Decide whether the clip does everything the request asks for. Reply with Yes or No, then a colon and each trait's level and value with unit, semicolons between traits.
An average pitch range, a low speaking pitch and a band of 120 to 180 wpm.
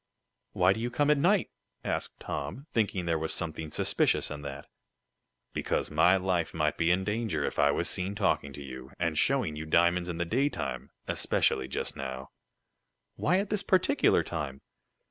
No: wide, 6.5 semitones; very low, 85 Hz; average, 175 wpm